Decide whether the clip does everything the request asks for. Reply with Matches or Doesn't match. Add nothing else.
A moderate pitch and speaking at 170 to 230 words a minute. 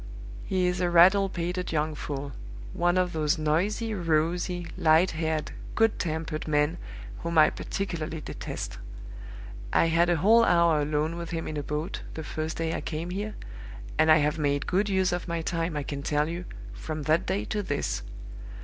Matches